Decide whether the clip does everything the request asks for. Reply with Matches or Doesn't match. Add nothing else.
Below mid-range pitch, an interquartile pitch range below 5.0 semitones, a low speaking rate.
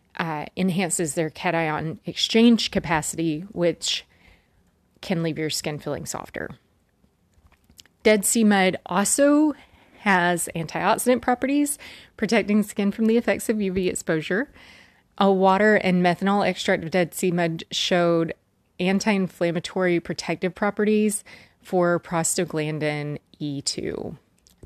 Doesn't match